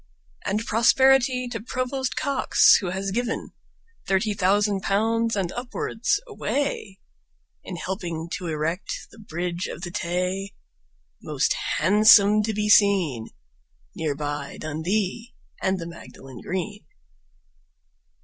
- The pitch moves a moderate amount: Yes, average, 4.4 semitones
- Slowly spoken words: Yes, slow, 115 wpm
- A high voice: Yes, high, 200 Hz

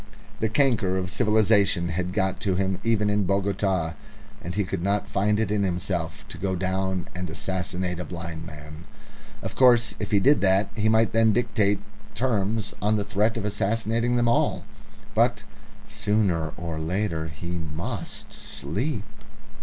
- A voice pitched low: Yes, low, 100 Hz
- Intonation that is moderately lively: Yes, average, 3.3 semitones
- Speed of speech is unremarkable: Yes, average, 160 wpm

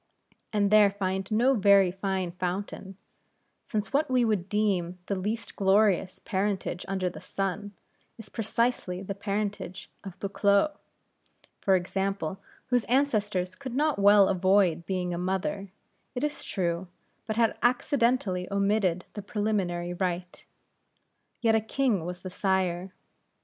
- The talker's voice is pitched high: Yes, high, 195 Hz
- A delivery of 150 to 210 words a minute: No, slow, 135 wpm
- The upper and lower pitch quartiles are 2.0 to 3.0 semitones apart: Yes, narrow, 2.5 semitones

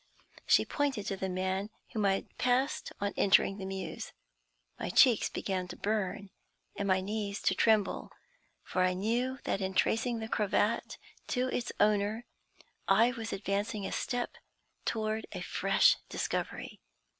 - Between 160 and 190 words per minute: No, average, 150 wpm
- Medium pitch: No, high, 210 Hz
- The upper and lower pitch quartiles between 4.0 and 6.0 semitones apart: No, average, 2.9 semitones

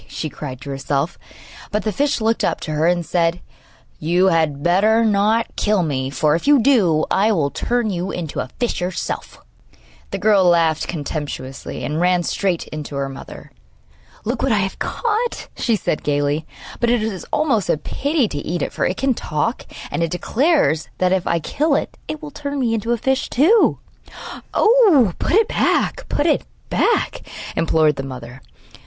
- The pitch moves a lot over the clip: Yes, wide, 7.5 semitones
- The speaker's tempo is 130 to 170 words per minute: No, average, 185 wpm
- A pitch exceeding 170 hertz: Yes, medium, 185 Hz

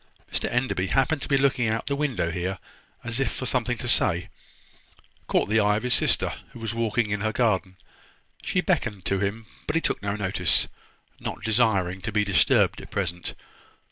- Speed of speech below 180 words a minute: No, average, 195 wpm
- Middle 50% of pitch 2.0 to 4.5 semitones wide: Yes, average, 4.1 semitones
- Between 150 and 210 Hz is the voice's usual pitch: No, low, 110 Hz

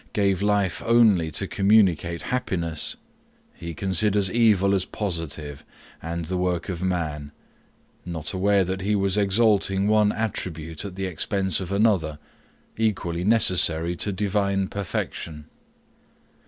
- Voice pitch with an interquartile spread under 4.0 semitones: Yes, average, 3.3 semitones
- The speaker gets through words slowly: Yes, slow, 125 wpm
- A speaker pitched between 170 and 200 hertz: No, very low, 95 Hz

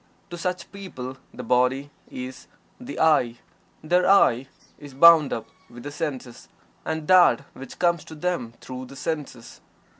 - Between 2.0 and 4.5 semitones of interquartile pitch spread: No, average, 5.1 semitones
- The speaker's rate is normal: Yes, average, 150 wpm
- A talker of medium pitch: Yes, medium, 145 Hz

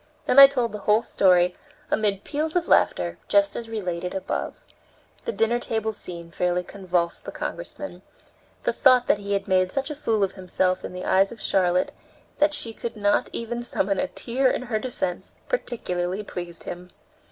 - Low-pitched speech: No, high, 205 Hz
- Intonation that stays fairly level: No, average, 4.9 semitones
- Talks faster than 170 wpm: Yes, average, 180 wpm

